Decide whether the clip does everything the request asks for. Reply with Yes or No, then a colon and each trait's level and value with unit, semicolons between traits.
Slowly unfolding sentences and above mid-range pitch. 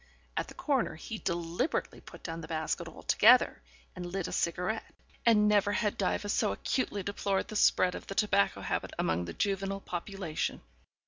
No: average, 170 wpm; high, 195 Hz